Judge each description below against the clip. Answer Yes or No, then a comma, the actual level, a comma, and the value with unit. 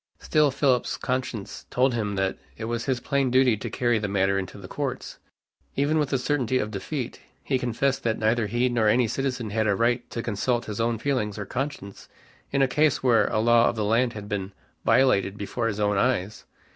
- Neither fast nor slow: No, fast, 210 wpm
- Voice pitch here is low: Yes, low, 120 Hz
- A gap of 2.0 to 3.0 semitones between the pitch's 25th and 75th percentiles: No, average, 3.5 semitones